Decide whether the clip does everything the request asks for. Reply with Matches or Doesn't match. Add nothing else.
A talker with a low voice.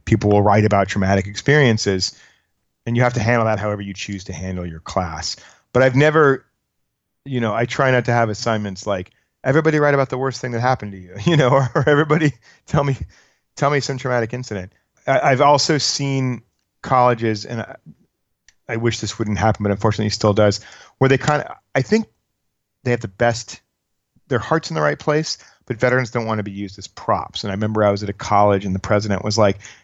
Matches